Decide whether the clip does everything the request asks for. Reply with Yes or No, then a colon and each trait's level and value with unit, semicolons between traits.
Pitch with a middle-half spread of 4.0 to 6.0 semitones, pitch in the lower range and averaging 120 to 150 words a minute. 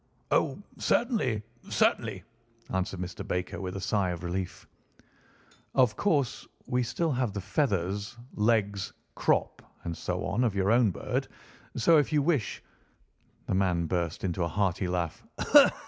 Yes: average, 5.1 semitones; low, 100 Hz; average, 145 wpm